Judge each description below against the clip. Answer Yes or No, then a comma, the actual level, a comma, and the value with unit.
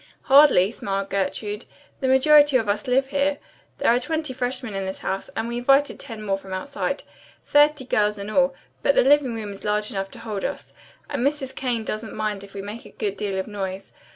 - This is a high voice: Yes, high, 225 Hz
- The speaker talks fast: Yes, fast, 210 wpm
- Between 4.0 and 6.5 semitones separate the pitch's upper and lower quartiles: Yes, average, 5.2 semitones